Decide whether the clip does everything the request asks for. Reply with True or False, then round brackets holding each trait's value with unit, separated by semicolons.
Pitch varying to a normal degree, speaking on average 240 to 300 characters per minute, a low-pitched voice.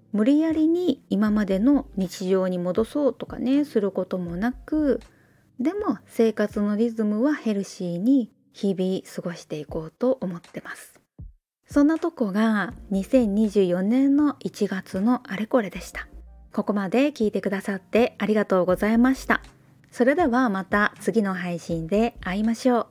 False (5.0 semitones; 295 characters per minute; 215 Hz)